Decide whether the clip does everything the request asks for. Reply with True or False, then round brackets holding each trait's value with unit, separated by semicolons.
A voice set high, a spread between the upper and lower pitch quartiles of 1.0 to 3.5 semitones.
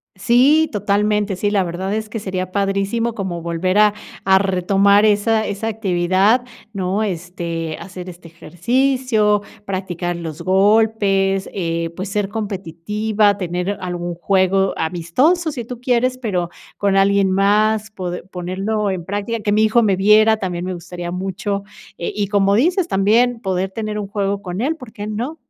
True (200 Hz; 2.9 semitones)